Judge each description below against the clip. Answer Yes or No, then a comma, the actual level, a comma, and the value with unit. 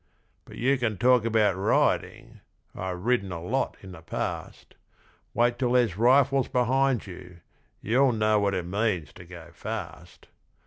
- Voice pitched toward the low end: Yes, low, 110 Hz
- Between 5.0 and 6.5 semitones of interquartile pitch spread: Yes, average, 5.3 semitones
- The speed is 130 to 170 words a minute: Yes, average, 150 wpm